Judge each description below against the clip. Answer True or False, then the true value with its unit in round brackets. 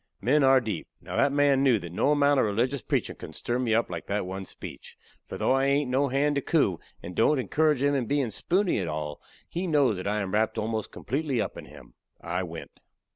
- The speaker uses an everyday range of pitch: False (6.0 semitones)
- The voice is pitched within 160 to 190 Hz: False (125 Hz)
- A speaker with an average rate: False (235 wpm)